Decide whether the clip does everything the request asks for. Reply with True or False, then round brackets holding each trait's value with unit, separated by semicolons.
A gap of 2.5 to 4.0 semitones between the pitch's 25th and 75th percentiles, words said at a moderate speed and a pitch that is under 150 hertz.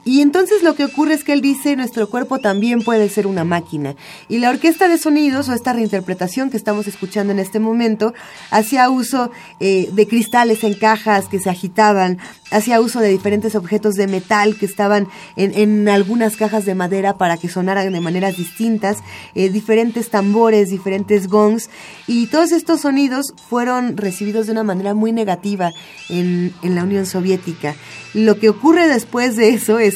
False (3.4 semitones; 180 wpm; 215 Hz)